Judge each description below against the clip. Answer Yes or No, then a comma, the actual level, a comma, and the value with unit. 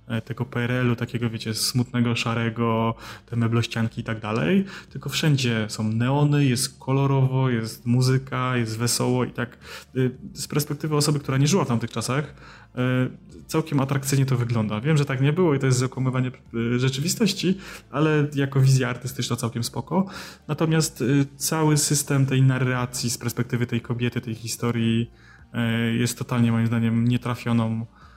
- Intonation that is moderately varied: Yes, average, 3.0 semitones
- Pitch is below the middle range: Yes, low, 125 Hz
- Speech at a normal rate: Yes, average, 145 wpm